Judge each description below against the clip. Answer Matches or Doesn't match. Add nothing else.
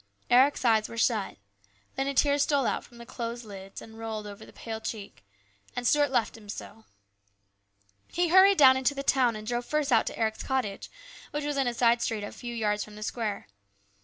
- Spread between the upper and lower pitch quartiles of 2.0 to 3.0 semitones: Doesn't match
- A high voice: Matches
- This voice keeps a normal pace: Doesn't match